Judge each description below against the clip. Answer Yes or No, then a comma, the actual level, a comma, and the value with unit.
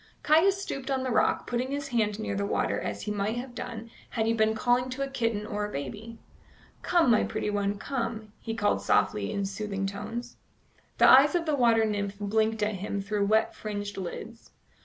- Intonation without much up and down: No, average, 3.1 semitones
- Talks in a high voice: Yes, high, 220 Hz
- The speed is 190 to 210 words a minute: Yes, average, 200 wpm